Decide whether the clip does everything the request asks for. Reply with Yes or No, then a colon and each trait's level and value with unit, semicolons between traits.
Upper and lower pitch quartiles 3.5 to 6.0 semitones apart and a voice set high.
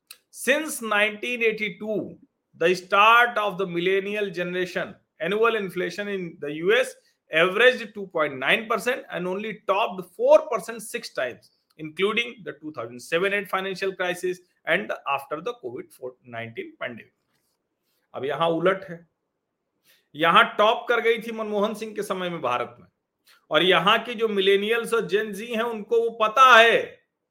Yes: average, 4.3 semitones; high, 205 Hz